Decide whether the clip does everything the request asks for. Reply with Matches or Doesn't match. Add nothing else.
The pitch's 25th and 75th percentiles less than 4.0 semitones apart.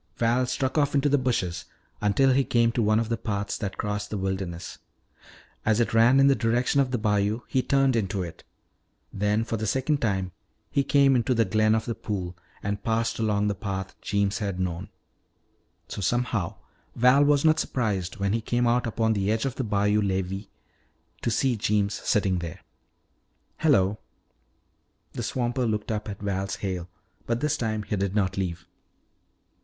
Matches